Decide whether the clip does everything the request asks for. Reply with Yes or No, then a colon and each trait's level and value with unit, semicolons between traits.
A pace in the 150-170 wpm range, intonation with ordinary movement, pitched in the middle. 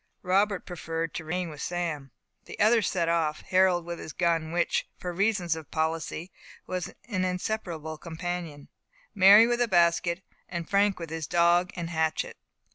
No: average, 160 wpm; narrow, 2.2 semitones; medium, 175 Hz